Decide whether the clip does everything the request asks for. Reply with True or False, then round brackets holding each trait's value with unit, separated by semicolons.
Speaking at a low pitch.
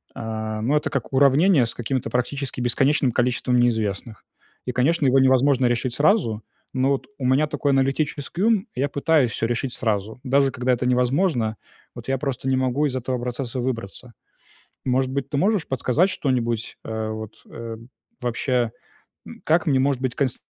True (130 Hz)